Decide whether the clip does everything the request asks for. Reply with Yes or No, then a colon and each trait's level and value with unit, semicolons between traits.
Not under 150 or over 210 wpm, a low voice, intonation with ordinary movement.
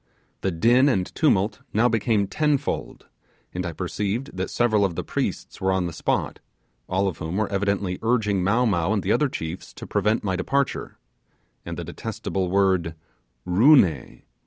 Yes: average, 170 wpm; low, 100 Hz; average, 3.7 semitones